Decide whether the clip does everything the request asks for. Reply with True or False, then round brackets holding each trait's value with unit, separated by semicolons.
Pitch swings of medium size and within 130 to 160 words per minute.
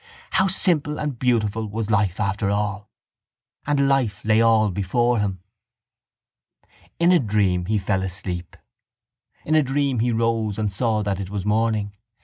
True (3.4 semitones; 150 wpm)